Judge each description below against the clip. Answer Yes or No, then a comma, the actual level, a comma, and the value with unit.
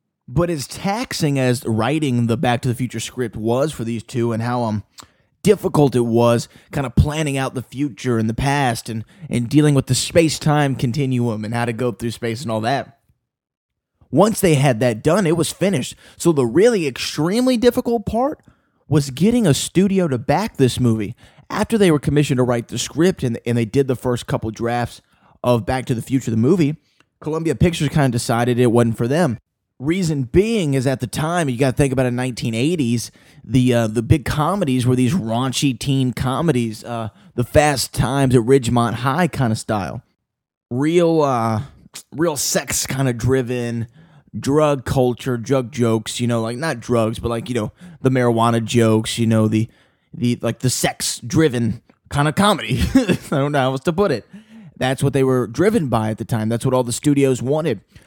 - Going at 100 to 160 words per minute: No, average, 195 wpm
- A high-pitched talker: No, low, 130 Hz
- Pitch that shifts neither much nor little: Yes, average, 4.1 semitones